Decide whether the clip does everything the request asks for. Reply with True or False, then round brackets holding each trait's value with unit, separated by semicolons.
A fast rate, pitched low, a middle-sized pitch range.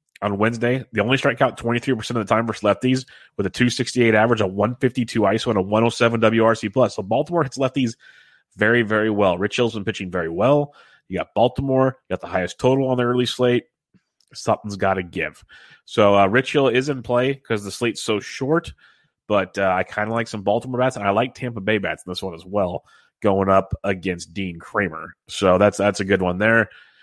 True (230 wpm; 110 Hz; 3.7 semitones)